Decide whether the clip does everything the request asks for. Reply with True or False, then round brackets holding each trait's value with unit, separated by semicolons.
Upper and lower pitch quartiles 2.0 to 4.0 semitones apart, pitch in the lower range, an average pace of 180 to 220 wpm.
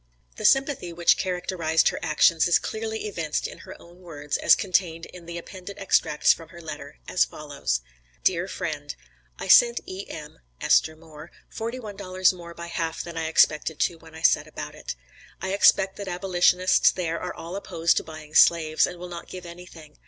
False (2.5 semitones; 170 Hz; 185 wpm)